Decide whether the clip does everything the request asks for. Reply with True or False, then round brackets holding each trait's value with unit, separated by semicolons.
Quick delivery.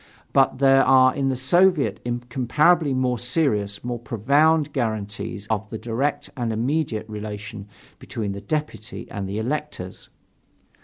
False (135 wpm)